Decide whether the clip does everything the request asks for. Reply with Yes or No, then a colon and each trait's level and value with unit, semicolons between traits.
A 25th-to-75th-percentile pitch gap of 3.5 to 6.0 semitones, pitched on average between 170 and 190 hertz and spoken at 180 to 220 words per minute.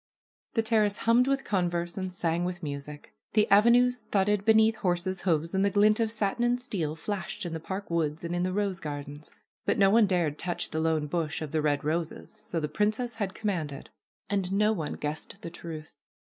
Yes: average, 4.7 semitones; medium, 185 Hz; average, 200 wpm